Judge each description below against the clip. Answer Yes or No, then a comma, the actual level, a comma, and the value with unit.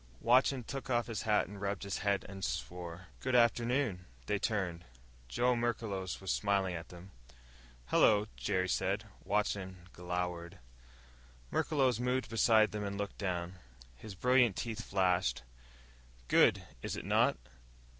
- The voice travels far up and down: No, average, 4.3 semitones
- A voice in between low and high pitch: No, low, 100 Hz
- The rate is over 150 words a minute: No, average, 140 wpm